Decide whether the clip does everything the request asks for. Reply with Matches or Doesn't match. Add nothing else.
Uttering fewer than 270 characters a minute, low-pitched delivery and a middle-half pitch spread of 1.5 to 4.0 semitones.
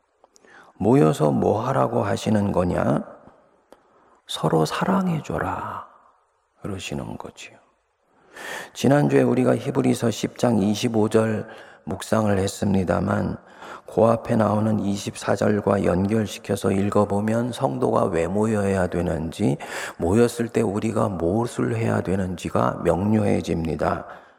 Matches